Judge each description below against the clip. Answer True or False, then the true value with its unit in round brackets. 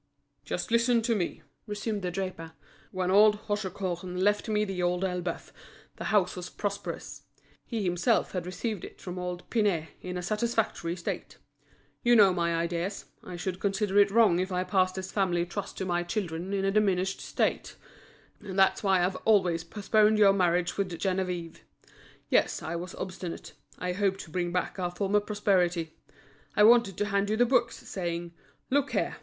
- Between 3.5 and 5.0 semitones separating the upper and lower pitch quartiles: False (2.7 semitones)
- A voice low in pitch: False (190 Hz)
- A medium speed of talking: True (175 wpm)